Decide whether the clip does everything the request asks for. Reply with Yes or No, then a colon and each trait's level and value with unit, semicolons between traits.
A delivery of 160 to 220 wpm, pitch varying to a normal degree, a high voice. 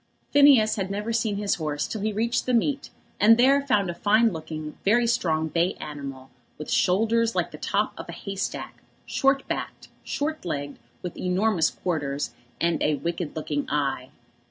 No: average, 175 wpm; wide, 6.7 semitones; high, 195 Hz